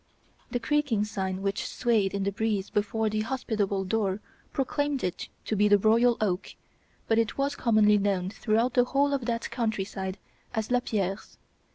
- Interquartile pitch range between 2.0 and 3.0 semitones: No, average, 3.4 semitones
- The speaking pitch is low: No, high, 215 Hz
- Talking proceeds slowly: No, average, 170 wpm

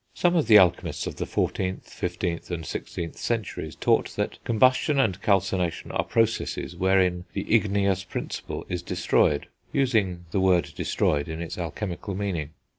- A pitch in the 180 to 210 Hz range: No, very low, 95 Hz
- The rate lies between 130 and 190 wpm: Yes, average, 150 wpm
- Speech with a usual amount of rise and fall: Yes, average, 3.5 semitones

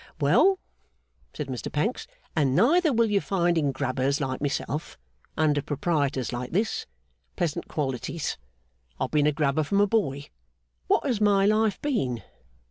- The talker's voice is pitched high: No, medium, 155 Hz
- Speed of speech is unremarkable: Yes, average, 145 wpm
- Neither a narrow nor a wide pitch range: No, wide, 6.9 semitones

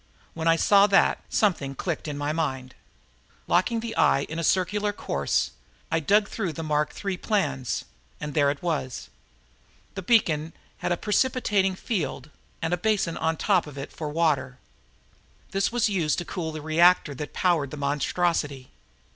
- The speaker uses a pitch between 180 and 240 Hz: No, medium, 165 Hz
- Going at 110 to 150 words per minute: No, average, 165 wpm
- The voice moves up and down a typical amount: Yes, average, 4.7 semitones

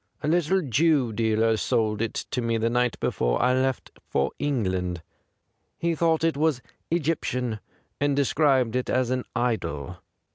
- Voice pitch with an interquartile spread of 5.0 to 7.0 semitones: No, average, 4.5 semitones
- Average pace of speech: Yes, average, 145 wpm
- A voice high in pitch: No, low, 125 Hz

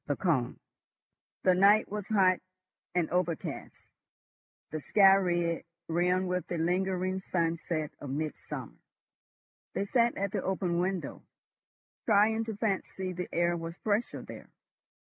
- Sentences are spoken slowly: Yes, slow, 130 wpm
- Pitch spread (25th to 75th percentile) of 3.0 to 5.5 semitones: No, narrow, 2.5 semitones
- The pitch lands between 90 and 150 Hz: No, medium, 180 Hz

